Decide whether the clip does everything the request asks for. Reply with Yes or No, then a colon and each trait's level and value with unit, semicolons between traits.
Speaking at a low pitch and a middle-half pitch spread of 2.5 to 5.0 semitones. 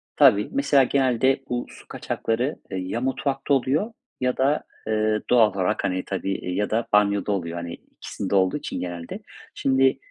No: low, 115 Hz; wide, 5.5 semitones